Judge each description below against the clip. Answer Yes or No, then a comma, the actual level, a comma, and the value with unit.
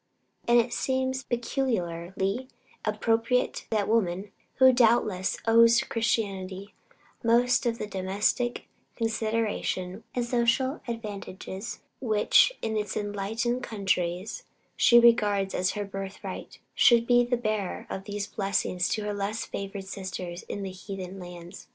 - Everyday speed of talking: No, slow, 120 wpm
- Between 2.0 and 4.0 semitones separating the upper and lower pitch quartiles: Yes, average, 3.5 semitones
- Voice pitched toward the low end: No, high, 215 Hz